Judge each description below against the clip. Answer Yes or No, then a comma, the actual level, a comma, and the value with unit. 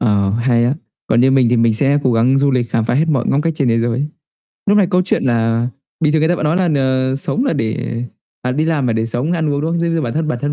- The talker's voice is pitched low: Yes, low, 130 Hz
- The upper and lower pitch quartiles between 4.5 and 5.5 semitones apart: Yes, average, 4.8 semitones